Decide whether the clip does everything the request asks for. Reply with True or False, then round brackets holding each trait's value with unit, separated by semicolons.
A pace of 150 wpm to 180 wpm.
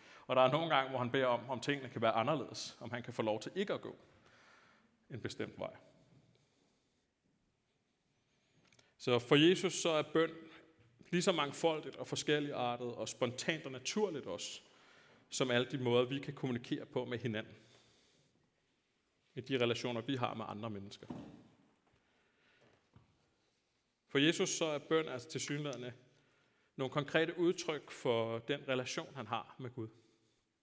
True (155 wpm)